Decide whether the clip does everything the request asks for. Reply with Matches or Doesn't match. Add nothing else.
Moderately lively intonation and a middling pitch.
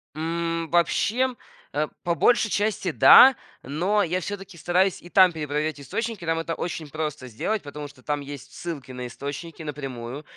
Matches